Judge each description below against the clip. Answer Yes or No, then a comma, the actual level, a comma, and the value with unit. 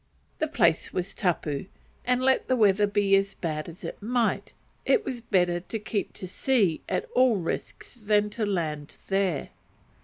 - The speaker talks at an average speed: Yes, average, 165 wpm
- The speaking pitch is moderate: No, high, 200 Hz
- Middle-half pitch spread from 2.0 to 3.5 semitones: No, average, 4.7 semitones